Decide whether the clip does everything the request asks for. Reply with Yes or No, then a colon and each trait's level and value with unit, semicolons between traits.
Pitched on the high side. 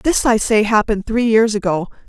Yes: high, 215 Hz